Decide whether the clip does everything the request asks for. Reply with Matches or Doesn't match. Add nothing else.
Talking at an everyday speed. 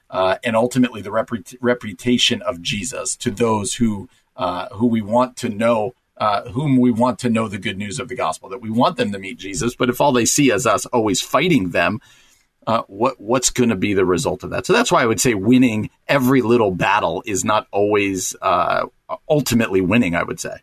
Doesn't match